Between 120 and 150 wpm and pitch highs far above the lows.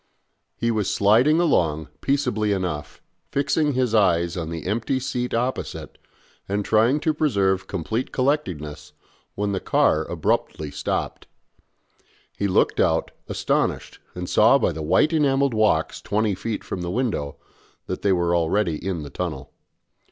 Yes: average, 145 wpm; wide, 6.6 semitones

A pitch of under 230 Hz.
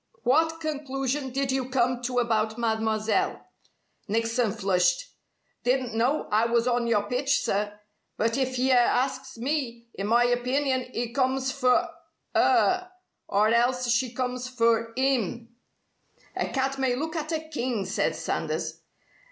No: very high, 250 Hz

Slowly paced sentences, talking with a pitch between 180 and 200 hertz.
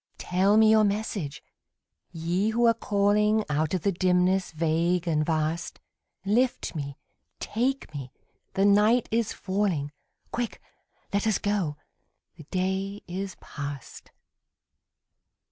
Yes: slow, 120 wpm; high, 190 Hz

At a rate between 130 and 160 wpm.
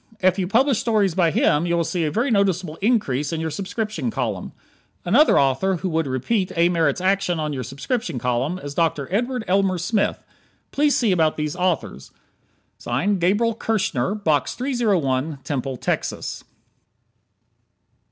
Yes: average, 150 wpm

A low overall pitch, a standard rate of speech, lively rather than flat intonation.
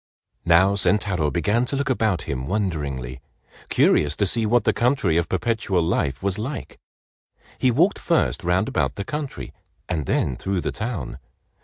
Yes: low, 100 Hz; average, 160 wpm; wide, 6.3 semitones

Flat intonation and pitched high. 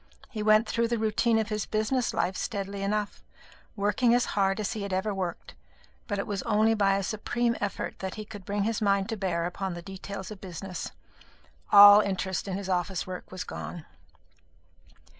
Yes: narrow, 2.1 semitones; high, 200 Hz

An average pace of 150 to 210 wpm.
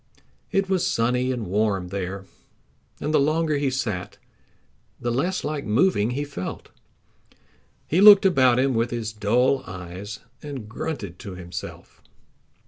No: slow, 135 wpm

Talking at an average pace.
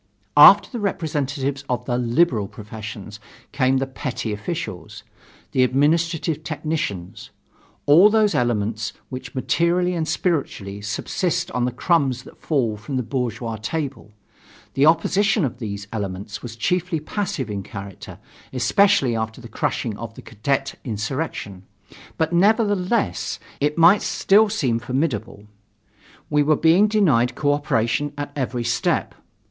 No: slow, 130 wpm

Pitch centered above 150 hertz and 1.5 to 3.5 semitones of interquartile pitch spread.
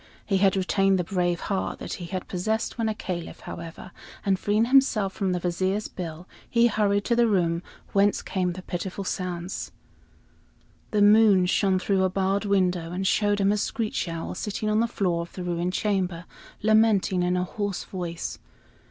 Yes: high, 190 Hz; narrow, 2.5 semitones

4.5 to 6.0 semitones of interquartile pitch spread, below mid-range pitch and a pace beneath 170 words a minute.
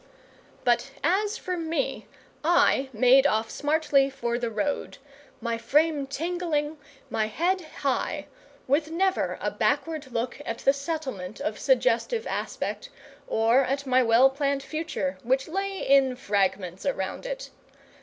No: average, 5.1 semitones; very high, 275 Hz; slow, 135 wpm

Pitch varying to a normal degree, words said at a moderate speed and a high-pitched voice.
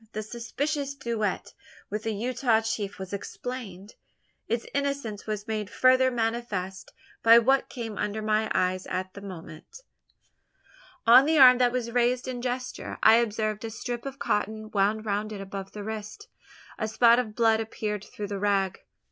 Yes: average, 3.0 semitones; average, 165 wpm; high, 220 Hz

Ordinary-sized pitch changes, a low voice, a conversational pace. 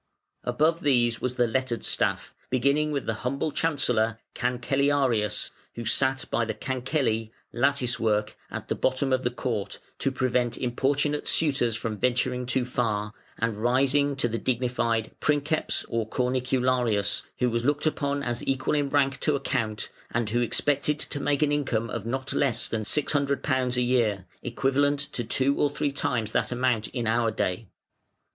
Yes: average, 3.2 semitones; low, 125 Hz; average, 160 wpm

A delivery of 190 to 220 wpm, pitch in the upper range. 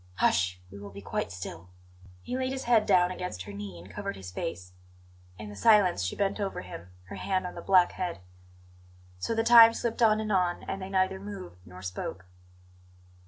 No: average, 200 wpm; medium, 180 Hz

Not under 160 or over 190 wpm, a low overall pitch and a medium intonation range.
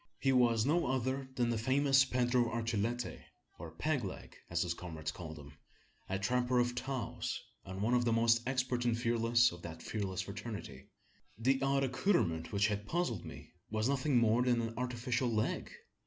Yes: average, 175 wpm; low, 120 Hz; average, 3.7 semitones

